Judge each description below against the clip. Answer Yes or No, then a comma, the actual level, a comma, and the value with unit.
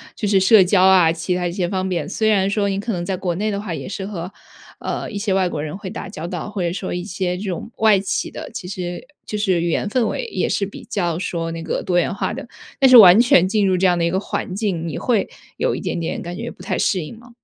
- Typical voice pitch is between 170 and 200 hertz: Yes, high, 190 Hz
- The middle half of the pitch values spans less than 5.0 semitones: Yes, average, 2.7 semitones